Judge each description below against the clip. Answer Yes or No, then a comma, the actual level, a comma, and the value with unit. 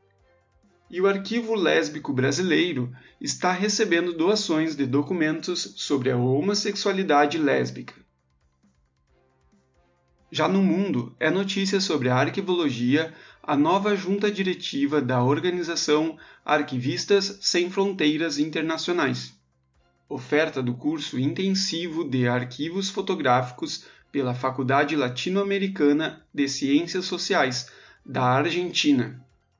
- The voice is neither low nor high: Yes, medium, 150 Hz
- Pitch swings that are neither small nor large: No, wide, 6.4 semitones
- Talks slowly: Yes, slow, 95 wpm